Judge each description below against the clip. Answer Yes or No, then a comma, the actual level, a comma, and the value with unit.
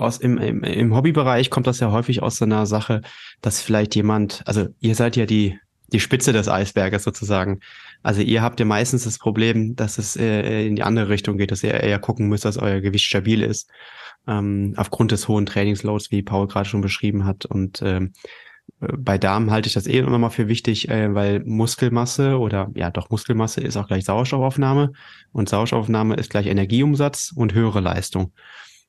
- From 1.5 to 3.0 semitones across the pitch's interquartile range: Yes, narrow, 2.6 semitones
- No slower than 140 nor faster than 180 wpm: No, fast, 190 wpm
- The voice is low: Yes, low, 110 Hz